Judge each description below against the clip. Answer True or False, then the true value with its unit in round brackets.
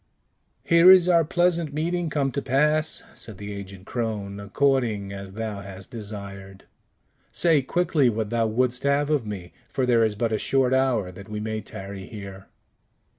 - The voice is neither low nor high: False (115 Hz)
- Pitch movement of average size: False (6.1 semitones)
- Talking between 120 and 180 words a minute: True (170 wpm)